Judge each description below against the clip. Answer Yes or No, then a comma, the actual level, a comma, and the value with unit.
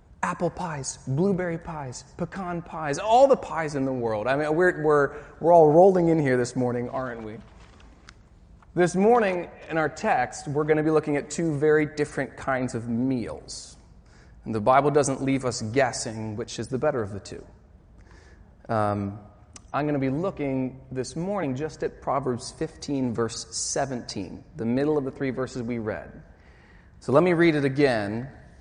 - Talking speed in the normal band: Yes, average, 175 wpm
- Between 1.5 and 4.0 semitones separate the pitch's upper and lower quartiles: No, average, 5.2 semitones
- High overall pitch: No, low, 135 Hz